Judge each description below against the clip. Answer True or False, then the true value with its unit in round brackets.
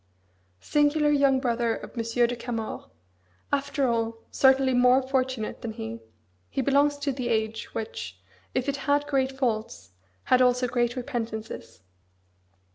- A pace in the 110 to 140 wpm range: True (135 wpm)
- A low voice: False (250 Hz)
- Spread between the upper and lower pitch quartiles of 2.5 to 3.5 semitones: True (3.0 semitones)